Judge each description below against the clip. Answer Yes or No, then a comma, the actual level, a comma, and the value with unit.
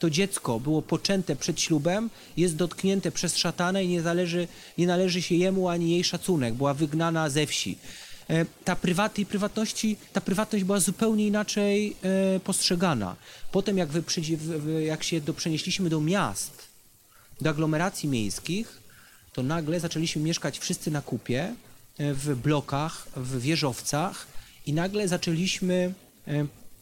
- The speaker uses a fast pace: No, average, 130 wpm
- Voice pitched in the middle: Yes, medium, 170 Hz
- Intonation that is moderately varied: Yes, average, 3.4 semitones